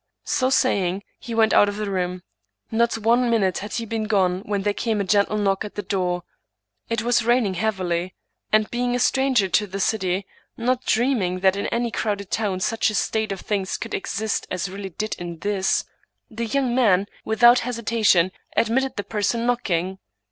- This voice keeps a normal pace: Yes, average, 190 wpm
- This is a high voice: Yes, high, 210 Hz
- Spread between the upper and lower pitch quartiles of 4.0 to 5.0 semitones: No, average, 3.5 semitones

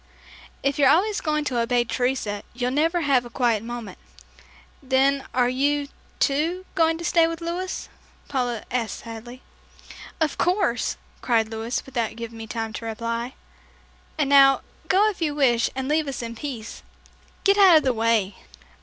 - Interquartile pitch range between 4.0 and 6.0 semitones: Yes, average, 4.7 semitones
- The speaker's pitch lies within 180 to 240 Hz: No, very high, 260 Hz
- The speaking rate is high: No, average, 165 wpm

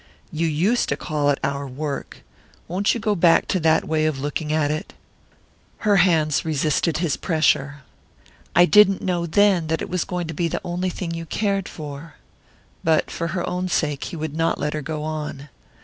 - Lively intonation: No, average, 2.9 semitones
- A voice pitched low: No, medium, 160 Hz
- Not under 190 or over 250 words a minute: Yes, average, 195 wpm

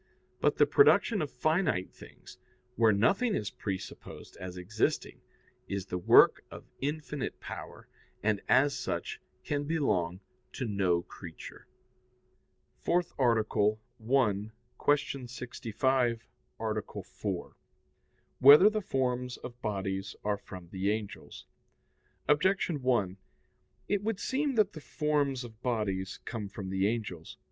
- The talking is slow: Yes, slow, 125 wpm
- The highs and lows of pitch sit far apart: Yes, wide, 6.6 semitones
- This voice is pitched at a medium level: No, low, 115 Hz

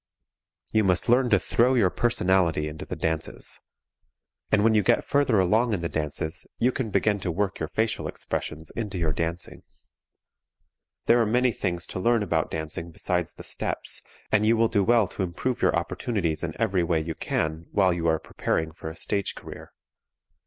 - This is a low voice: Yes, very low, 95 Hz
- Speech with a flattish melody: No, average, 5.1 semitones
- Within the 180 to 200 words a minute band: Yes, average, 185 wpm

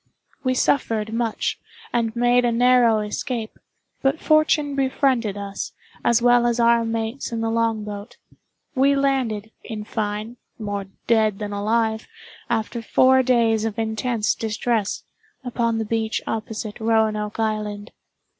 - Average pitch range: No, narrow, 2.1 semitones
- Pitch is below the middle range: No, high, 225 Hz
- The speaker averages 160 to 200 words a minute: No, slow, 135 wpm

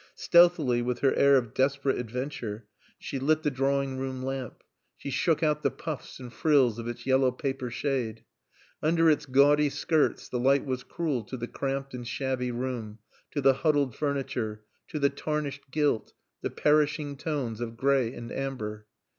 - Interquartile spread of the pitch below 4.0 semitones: Yes, average, 2.8 semitones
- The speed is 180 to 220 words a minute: No, average, 170 wpm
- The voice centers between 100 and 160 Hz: Yes, low, 135 Hz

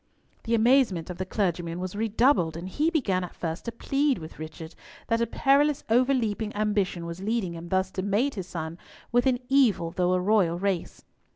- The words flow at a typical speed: Yes, average, 190 wpm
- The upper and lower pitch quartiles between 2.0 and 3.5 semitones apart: No, average, 5.3 semitones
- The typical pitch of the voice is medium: No, high, 200 Hz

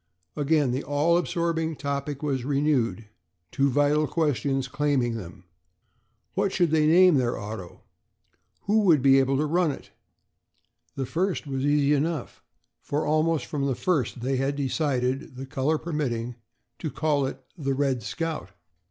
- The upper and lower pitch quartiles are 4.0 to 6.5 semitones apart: No, average, 3.0 semitones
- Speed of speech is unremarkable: Yes, average, 150 wpm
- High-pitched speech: No, medium, 145 Hz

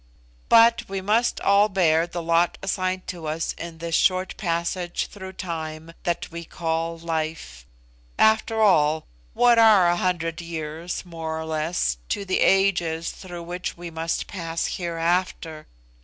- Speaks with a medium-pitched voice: Yes, medium, 170 Hz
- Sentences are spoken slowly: No, average, 145 wpm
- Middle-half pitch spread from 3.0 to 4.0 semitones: No, narrow, 2.4 semitones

